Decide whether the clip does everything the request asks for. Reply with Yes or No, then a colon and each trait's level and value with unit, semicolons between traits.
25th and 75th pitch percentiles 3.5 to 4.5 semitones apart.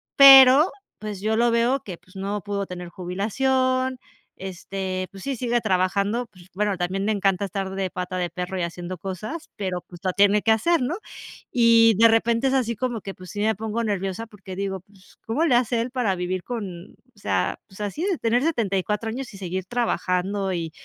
Yes: average, 4.0 semitones